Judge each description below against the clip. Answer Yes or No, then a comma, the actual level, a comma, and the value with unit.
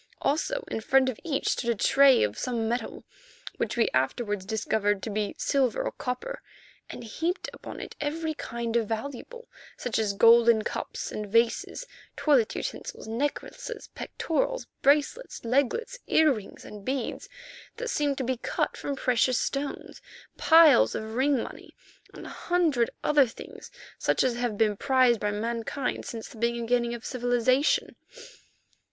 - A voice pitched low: No, high, 245 Hz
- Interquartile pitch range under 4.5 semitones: Yes, average, 4.1 semitones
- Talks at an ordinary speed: Yes, average, 150 wpm